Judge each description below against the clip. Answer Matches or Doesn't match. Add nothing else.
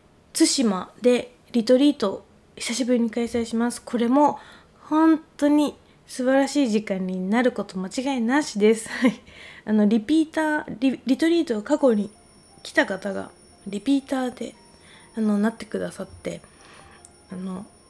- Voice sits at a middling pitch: Doesn't match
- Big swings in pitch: Doesn't match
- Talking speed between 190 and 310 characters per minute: Matches